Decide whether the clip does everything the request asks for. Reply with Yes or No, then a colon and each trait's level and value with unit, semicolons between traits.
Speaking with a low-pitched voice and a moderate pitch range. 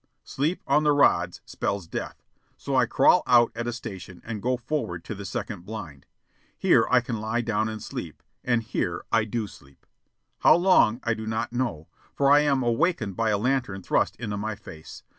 Yes: low, 110 Hz; average, 3.9 semitones